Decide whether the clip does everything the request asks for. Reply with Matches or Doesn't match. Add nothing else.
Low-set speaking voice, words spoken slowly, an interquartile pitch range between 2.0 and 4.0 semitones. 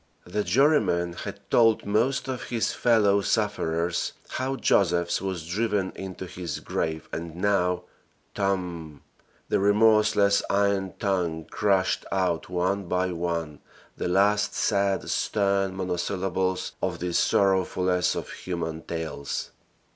Matches